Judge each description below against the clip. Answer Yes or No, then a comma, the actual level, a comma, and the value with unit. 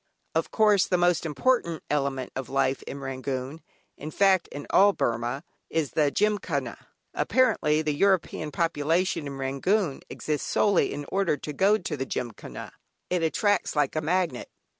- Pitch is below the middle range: No, medium, 155 Hz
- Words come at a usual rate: Yes, average, 155 wpm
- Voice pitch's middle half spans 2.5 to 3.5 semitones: No, average, 5.3 semitones